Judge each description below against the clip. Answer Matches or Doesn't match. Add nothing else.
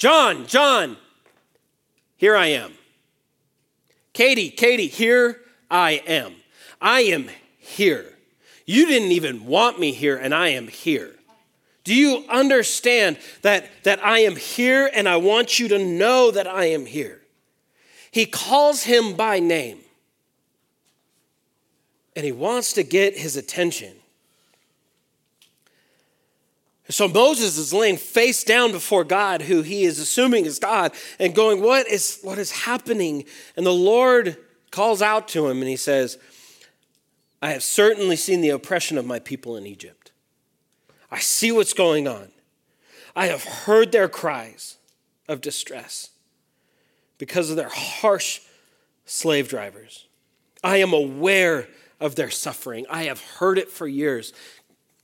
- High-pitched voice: Matches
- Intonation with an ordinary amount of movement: Doesn't match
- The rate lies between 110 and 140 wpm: Matches